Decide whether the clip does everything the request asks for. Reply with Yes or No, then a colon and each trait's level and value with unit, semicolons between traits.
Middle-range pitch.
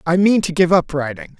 Yes: medium, 175 Hz